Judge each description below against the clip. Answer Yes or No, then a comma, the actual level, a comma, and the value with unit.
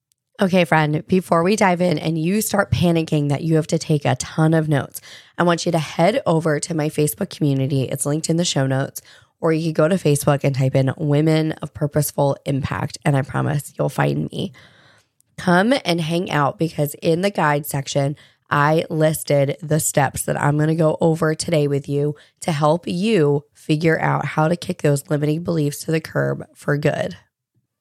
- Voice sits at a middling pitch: Yes, medium, 150 Hz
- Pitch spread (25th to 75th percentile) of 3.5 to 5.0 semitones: No, narrow, 2.6 semitones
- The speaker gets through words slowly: No, average, 200 wpm